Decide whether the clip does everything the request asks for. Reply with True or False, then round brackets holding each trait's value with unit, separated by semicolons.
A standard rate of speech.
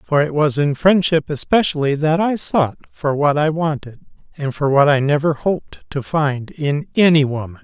True (190 wpm)